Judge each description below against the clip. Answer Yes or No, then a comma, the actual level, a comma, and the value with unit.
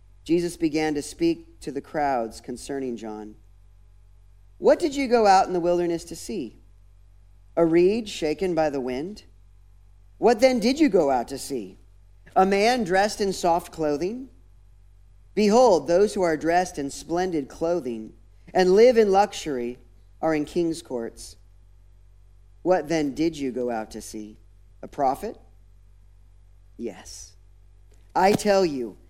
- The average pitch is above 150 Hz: No, low, 125 Hz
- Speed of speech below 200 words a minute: Yes, average, 140 wpm